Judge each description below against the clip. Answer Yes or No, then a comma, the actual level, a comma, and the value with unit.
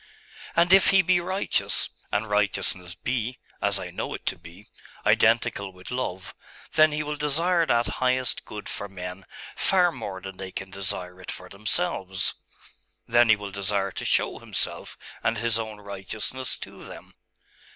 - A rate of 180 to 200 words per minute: No, average, 160 wpm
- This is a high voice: No, low, 105 Hz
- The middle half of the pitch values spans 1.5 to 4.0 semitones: No, average, 5.2 semitones